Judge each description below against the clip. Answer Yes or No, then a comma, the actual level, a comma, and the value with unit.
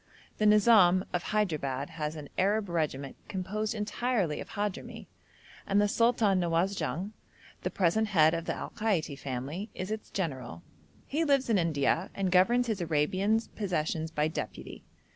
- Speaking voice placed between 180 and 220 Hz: Yes, medium, 185 Hz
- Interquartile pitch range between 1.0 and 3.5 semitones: No, average, 5.0 semitones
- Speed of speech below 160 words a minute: Yes, average, 150 wpm